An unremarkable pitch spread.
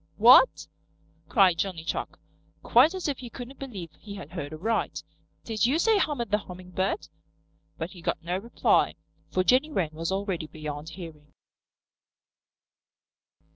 No: wide, 6.7 semitones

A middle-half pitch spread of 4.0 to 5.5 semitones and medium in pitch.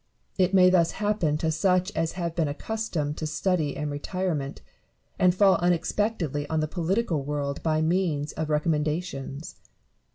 No: average, 3.5 semitones; medium, 165 Hz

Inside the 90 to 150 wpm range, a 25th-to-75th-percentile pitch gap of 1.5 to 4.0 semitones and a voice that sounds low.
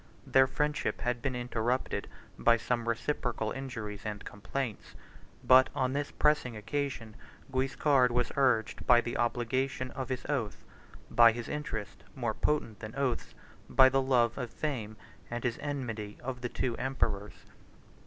Yes: average, 145 wpm; average, 2.8 semitones; low, 125 Hz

